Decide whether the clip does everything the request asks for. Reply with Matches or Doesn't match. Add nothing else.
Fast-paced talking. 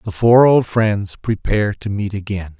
Doesn't match